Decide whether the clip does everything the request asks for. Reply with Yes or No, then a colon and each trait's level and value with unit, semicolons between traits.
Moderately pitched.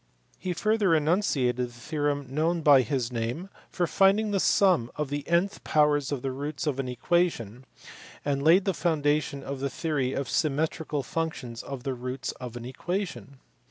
Yes: medium, 145 Hz